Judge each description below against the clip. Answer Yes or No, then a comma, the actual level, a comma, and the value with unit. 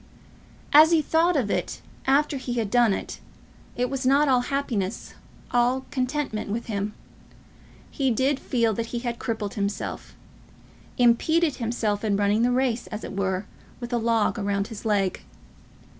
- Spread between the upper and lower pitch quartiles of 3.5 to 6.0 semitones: Yes, average, 3.9 semitones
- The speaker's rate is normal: Yes, average, 160 wpm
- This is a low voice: No, high, 240 Hz